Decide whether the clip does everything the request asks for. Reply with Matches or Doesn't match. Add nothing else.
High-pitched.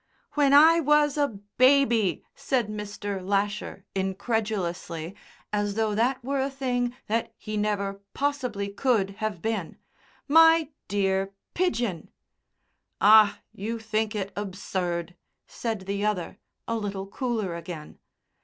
Matches